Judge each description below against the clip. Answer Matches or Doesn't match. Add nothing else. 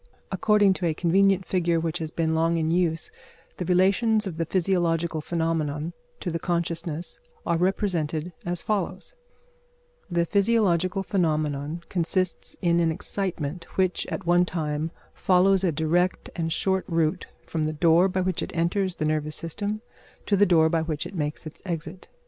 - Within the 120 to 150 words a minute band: Doesn't match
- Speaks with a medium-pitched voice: Matches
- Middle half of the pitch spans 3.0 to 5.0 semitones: Doesn't match